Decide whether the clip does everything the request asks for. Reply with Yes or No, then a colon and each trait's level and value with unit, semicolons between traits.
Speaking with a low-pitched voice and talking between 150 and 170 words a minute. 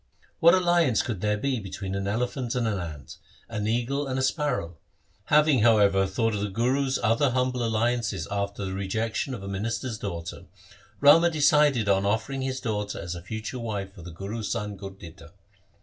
No: low, 110 Hz; average, 180 wpm